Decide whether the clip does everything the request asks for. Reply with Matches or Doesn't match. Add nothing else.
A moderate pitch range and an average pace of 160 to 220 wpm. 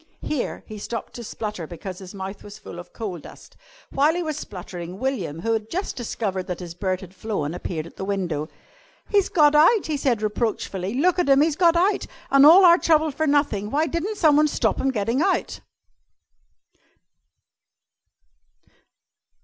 Doesn't match